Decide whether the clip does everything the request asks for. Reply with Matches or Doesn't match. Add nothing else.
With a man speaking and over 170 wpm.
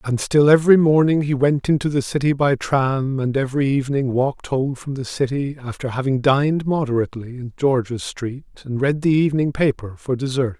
Matches